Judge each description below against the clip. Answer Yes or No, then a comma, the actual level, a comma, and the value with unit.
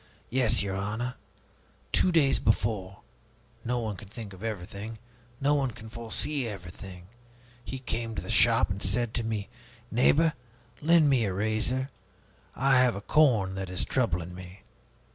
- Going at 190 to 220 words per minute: No, average, 155 wpm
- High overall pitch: No, low, 110 Hz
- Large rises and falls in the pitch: No, average, 4.7 semitones